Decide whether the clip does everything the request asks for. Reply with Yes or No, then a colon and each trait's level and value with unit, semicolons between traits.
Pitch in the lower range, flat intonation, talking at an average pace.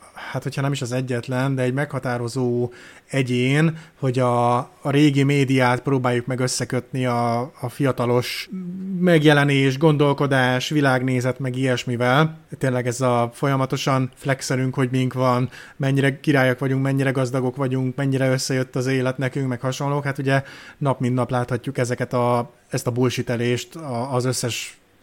Yes: low, 130 Hz; narrow, 1.9 semitones; average, 145 wpm